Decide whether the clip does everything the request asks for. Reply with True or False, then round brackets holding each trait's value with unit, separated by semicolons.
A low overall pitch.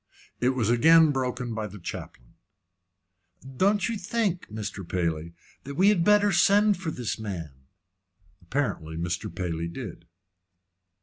True (120 Hz)